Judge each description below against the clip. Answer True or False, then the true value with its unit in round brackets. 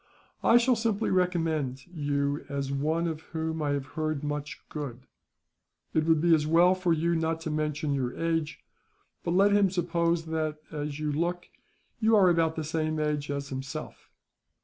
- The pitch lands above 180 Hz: False (160 Hz)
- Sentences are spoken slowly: False (170 wpm)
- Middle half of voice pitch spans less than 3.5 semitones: True (2.6 semitones)